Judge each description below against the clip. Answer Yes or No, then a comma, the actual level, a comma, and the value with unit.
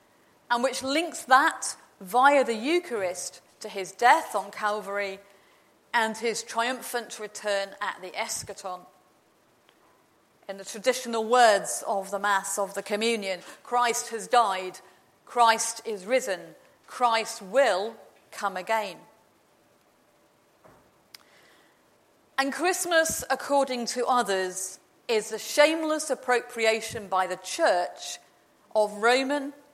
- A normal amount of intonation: Yes, average, 4.3 semitones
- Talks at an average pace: No, slow, 105 wpm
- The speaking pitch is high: Yes, high, 225 Hz